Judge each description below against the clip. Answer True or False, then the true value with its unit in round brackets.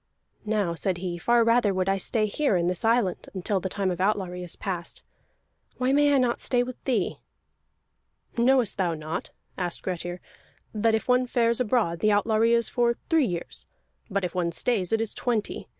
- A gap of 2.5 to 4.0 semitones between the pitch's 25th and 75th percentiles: False (4.7 semitones)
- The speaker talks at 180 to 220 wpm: True (185 wpm)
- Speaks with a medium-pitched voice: False (210 Hz)